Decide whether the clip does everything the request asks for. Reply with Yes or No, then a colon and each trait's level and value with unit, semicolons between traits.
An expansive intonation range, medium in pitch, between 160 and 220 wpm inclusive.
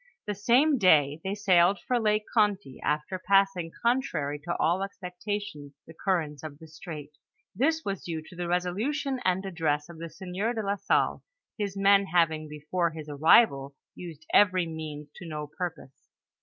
No: average, 4.4 semitones; medium, 180 Hz; average, 165 wpm